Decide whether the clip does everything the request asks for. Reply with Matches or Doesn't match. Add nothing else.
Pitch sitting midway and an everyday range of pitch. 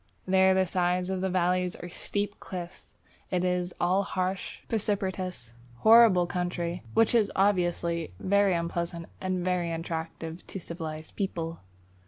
Doesn't match